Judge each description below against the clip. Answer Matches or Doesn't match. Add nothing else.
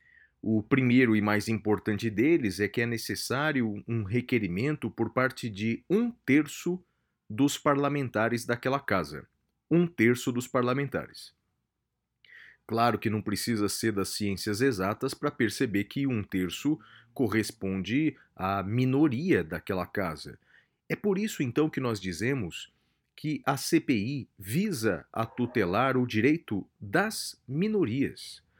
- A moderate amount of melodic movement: Matches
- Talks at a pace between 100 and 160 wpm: Matches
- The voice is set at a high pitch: Doesn't match